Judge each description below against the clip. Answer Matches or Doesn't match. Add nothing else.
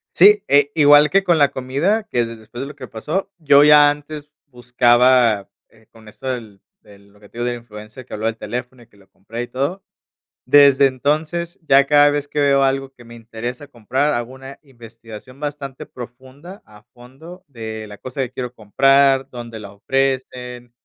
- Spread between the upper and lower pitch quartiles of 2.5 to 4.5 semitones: Matches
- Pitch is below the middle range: Matches